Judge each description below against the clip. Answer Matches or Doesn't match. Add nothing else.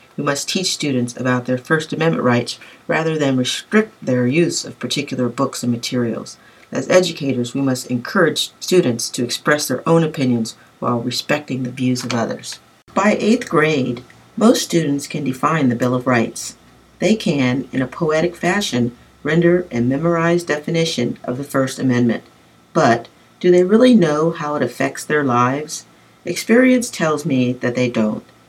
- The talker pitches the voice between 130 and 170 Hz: Matches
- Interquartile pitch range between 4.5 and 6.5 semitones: Matches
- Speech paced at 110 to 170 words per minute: Matches